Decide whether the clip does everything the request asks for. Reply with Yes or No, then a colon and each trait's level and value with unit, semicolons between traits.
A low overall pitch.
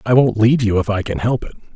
Yes: low, 110 Hz